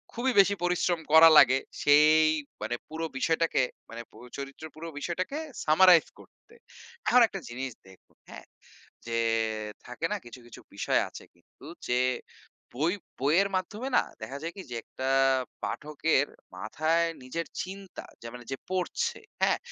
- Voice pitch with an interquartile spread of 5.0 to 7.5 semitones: Yes, wide, 5.5 semitones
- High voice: No, medium, 160 Hz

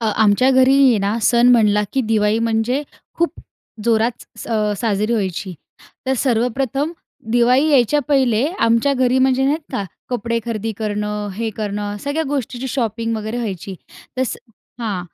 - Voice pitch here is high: Yes, high, 230 Hz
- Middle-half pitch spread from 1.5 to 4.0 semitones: Yes, average, 3.5 semitones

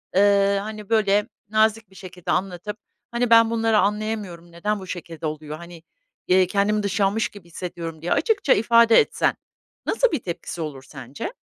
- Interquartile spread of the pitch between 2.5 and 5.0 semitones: Yes, average, 4.1 semitones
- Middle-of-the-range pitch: No, high, 200 Hz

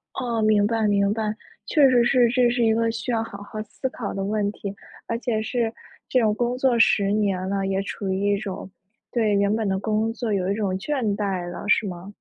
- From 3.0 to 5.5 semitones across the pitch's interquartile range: No, narrow, 2.5 semitones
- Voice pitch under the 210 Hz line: No, high, 215 Hz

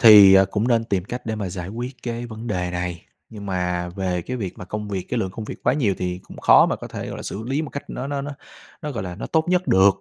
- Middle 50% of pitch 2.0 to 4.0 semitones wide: No, average, 4.7 semitones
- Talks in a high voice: No, low, 105 Hz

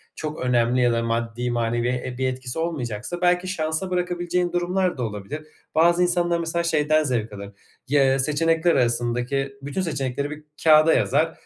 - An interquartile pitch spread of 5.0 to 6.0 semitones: Yes, wide, 5.5 semitones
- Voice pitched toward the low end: No, medium, 145 Hz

